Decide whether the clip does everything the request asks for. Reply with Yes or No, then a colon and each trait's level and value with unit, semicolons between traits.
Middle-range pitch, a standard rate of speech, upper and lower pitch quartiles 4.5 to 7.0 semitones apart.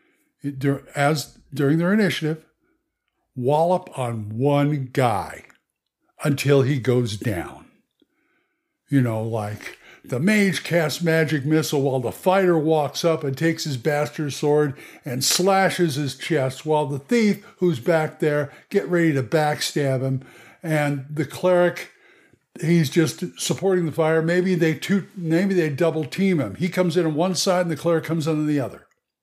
No: medium, 155 Hz; average, 155 wpm; average, 3.8 semitones